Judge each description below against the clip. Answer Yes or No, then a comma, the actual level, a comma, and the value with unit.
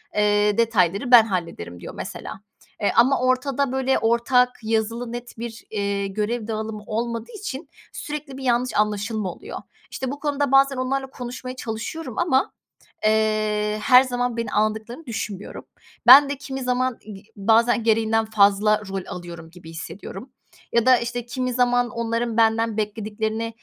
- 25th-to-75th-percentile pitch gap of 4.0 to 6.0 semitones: No, average, 3.0 semitones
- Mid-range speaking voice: No, high, 230 Hz